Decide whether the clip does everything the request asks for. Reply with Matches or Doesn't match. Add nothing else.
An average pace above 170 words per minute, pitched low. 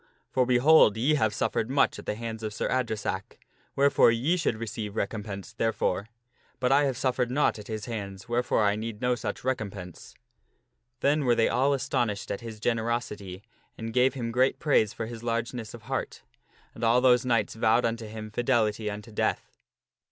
Matches